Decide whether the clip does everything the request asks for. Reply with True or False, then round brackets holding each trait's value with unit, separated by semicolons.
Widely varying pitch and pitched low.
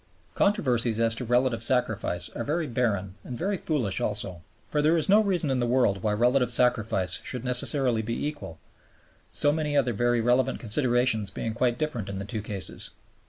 False (3.8 semitones; 120 Hz)